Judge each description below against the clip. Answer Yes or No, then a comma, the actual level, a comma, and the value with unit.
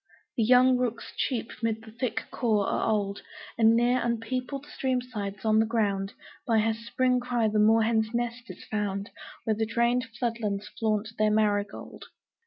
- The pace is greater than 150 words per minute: Yes, average, 175 wpm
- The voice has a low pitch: No, high, 225 Hz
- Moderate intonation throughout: No, narrow, 2.0 semitones